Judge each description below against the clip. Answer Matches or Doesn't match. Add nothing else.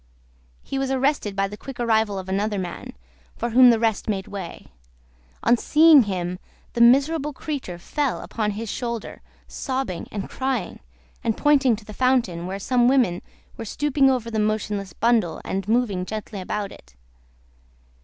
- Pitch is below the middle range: Doesn't match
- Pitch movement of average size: Matches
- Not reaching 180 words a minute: Matches